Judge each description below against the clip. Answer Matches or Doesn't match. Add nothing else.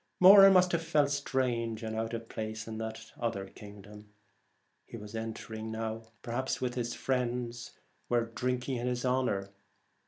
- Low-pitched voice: Matches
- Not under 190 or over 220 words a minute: Doesn't match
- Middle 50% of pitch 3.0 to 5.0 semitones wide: Doesn't match